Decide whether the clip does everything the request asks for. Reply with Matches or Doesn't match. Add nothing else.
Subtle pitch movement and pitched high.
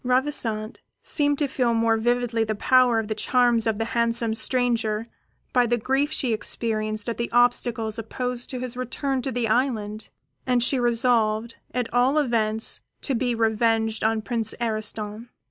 Matches